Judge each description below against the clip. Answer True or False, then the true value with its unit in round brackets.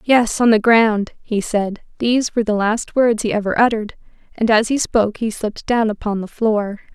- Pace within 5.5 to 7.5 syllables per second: False (5.3 syllables/s)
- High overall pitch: True (220 Hz)